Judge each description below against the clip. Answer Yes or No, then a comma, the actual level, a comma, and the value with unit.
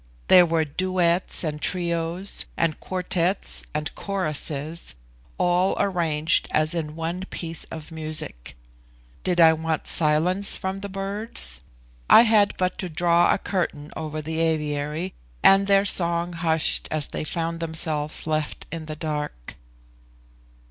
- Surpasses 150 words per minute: No, slow, 135 wpm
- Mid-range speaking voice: Yes, medium, 165 Hz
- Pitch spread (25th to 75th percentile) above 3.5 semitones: No, average, 2.9 semitones